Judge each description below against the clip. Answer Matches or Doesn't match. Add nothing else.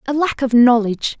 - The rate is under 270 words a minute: Matches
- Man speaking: Doesn't match